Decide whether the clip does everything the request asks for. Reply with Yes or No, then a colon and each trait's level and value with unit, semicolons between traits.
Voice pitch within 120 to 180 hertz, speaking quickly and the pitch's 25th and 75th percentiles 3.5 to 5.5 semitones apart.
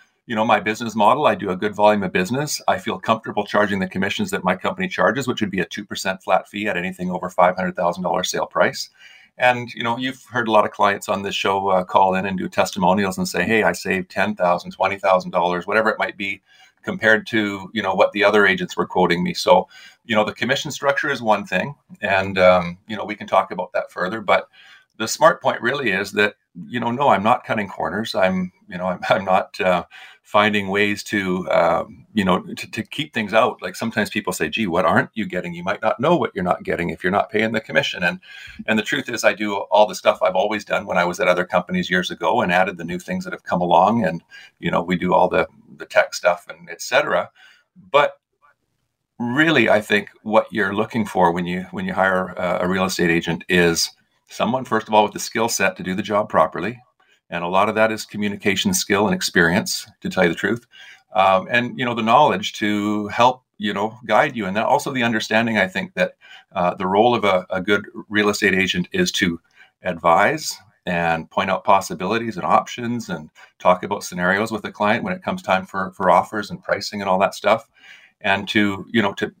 No: low, 105 Hz; fast, 230 wpm; average, 4.0 semitones